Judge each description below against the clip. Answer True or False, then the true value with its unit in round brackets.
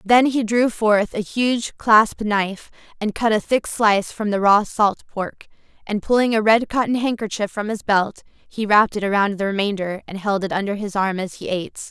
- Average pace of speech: False (210 wpm)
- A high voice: True (210 Hz)